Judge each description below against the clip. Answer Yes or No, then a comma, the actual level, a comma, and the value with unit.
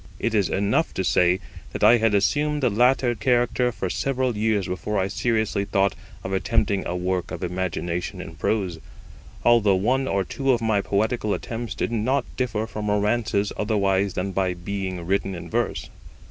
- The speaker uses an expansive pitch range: No, average, 3.7 semitones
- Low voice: Yes, low, 105 Hz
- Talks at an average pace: Yes, average, 175 wpm